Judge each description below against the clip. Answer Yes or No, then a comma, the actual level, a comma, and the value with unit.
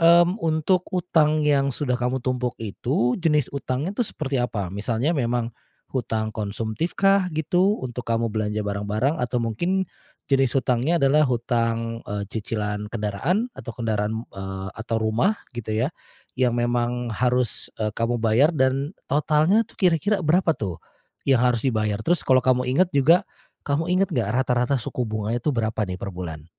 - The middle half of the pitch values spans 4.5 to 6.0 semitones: Yes, wide, 5.4 semitones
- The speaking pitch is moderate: No, low, 125 Hz